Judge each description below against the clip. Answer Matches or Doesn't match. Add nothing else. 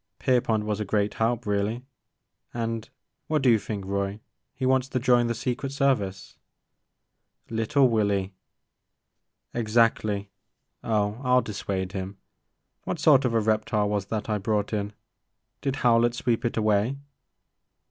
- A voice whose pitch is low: Matches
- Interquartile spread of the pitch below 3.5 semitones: Matches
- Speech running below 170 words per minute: Matches